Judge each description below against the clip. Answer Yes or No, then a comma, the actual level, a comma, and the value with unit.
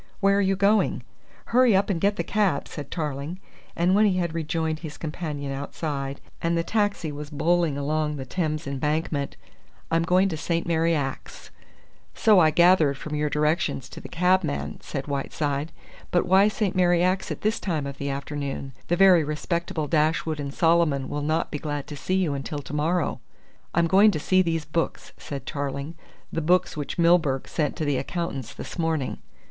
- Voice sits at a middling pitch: Yes, medium, 160 Hz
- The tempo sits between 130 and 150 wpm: No, average, 185 wpm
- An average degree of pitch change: Yes, average, 3.5 semitones